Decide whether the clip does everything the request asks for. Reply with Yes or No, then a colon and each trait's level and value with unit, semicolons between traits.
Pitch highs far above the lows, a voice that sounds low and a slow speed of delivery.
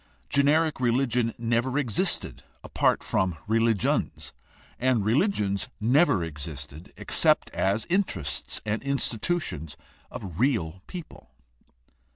Yes: wide, 6.6 semitones; low, 115 Hz; slow, 95 wpm